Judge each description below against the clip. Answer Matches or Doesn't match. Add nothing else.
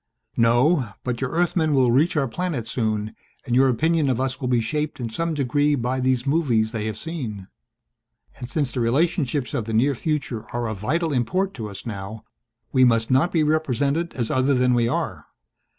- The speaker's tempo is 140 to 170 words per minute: Doesn't match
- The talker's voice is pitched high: Doesn't match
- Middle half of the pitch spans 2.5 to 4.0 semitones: Doesn't match